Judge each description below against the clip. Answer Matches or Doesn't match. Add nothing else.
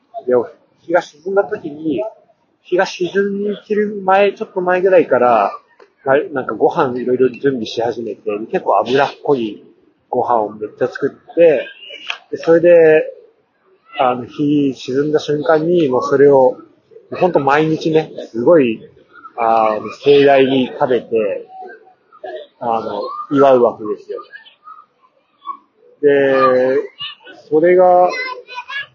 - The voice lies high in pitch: Matches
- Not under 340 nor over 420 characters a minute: Doesn't match